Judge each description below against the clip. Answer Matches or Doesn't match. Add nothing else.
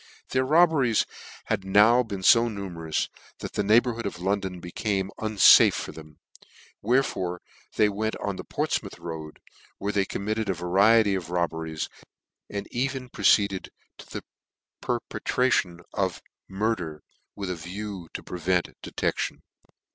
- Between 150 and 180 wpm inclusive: Doesn't match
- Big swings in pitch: Doesn't match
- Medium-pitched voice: Doesn't match